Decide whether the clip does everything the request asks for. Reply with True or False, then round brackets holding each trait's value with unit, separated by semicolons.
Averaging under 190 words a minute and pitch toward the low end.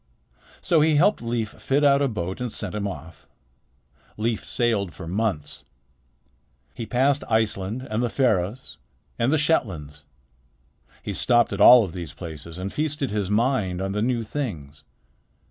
True (155 wpm; 110 Hz)